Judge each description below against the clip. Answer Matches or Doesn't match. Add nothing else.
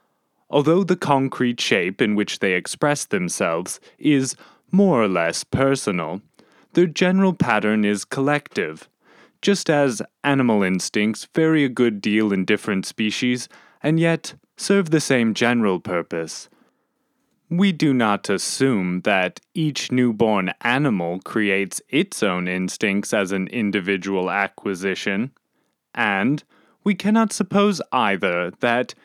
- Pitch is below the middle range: Matches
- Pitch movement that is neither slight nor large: Doesn't match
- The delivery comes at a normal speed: Doesn't match